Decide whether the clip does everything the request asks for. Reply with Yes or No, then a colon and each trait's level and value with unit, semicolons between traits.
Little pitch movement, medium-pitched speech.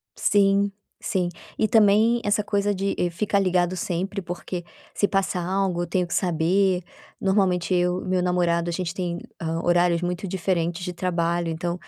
Yes: narrow, 2.2 semitones; medium, 180 Hz